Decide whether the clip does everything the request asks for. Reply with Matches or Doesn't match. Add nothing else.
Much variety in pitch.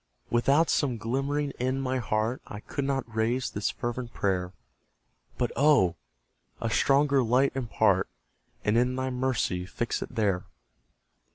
Doesn't match